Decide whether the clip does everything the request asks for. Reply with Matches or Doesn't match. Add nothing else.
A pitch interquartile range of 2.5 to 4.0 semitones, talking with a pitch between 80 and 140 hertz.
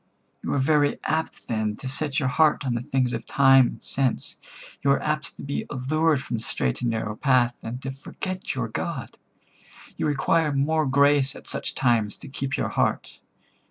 Matches